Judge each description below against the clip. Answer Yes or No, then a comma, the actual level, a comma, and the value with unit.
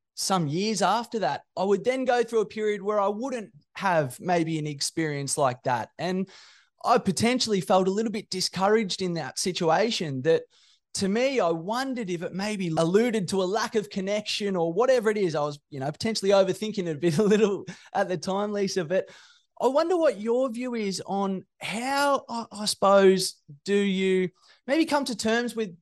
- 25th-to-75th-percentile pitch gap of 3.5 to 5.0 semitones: Yes, average, 3.8 semitones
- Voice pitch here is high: Yes, high, 200 Hz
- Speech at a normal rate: Yes, average, 190 wpm